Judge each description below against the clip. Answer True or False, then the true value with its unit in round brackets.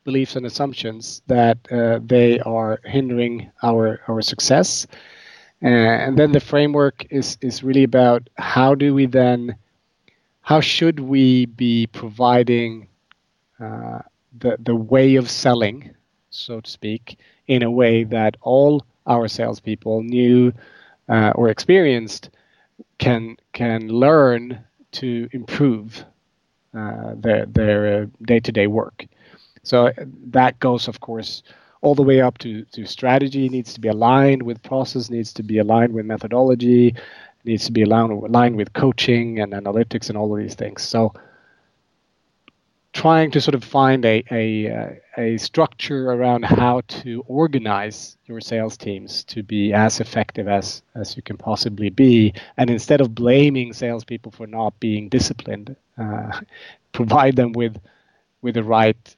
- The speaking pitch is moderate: False (120 Hz)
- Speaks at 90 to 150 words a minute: True (145 wpm)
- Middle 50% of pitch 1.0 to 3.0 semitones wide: True (2.6 semitones)